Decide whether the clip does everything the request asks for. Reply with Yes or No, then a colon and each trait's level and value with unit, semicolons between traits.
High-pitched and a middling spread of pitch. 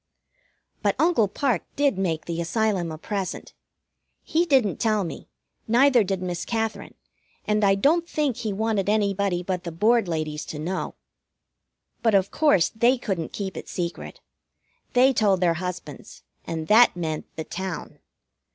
Yes: high, 200 Hz; average, 4.7 semitones